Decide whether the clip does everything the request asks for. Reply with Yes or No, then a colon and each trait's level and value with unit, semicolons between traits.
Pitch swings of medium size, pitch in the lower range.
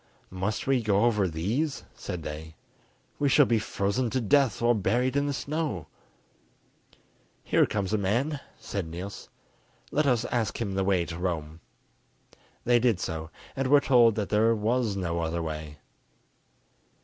No: wide, 5.7 semitones; low, 105 Hz